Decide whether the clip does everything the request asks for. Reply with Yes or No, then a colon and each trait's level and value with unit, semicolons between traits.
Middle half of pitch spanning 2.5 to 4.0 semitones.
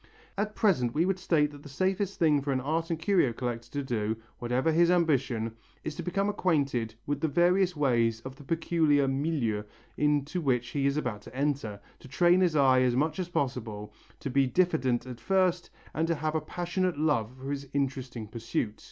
No: average, 5.0 semitones